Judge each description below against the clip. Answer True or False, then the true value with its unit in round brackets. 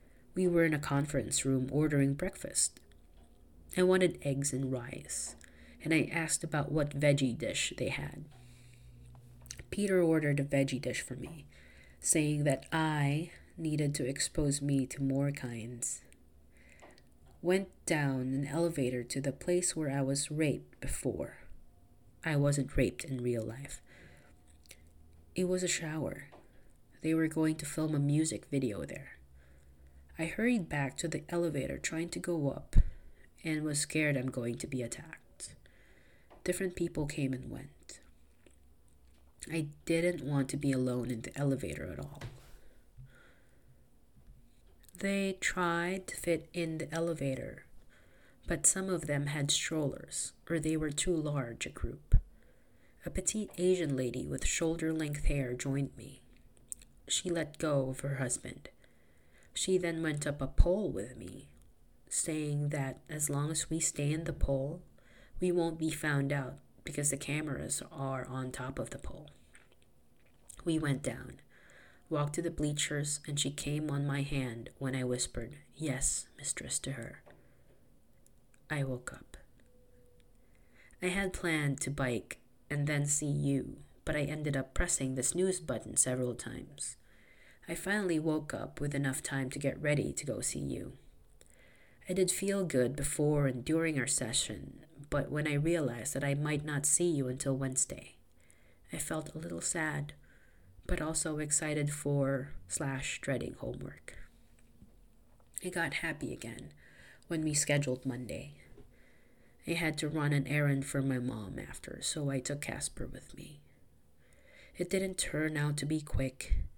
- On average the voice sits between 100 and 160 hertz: True (140 Hz)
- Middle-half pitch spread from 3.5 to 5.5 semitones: True (4.2 semitones)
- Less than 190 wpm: True (150 wpm)